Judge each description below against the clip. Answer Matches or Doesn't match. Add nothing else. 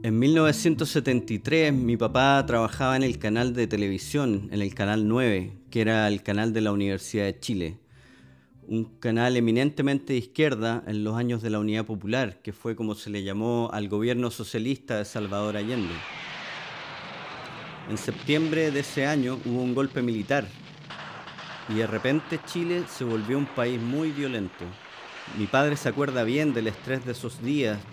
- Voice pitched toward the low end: Matches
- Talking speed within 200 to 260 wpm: Doesn't match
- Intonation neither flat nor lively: Matches